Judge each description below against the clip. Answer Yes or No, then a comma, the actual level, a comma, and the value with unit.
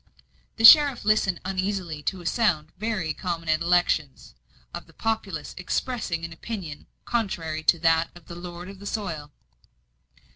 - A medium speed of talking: Yes, average, 150 wpm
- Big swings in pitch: No, average, 4.2 semitones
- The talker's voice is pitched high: No, medium, 175 Hz